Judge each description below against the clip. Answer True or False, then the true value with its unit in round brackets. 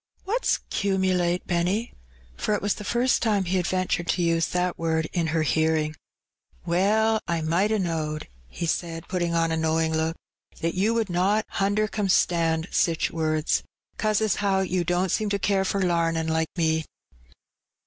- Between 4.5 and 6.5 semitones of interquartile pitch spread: False (3.4 semitones)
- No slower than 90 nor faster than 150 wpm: False (170 wpm)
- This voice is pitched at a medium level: True (175 Hz)